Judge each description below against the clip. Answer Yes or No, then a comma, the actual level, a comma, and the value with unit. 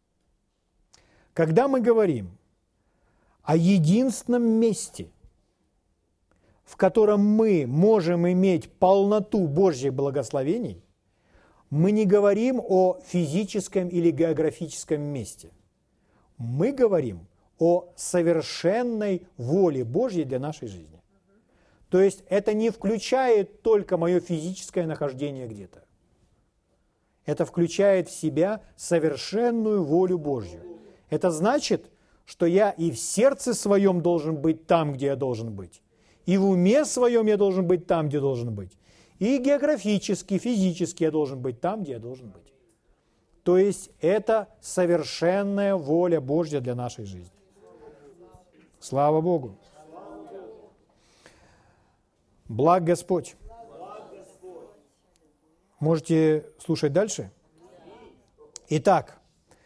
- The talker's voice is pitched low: No, medium, 175 Hz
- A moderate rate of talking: No, slow, 105 wpm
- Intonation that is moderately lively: No, wide, 6.0 semitones